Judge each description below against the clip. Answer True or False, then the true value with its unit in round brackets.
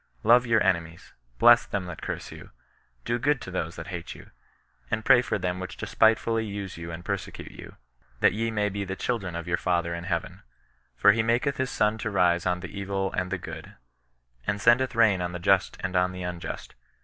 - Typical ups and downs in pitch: True (4.1 semitones)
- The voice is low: True (95 Hz)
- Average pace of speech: False (215 wpm)